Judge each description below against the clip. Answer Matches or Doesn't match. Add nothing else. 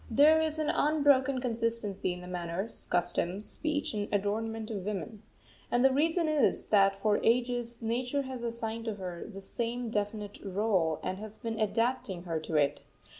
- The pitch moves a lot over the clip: Doesn't match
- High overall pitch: Matches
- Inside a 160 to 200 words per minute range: Matches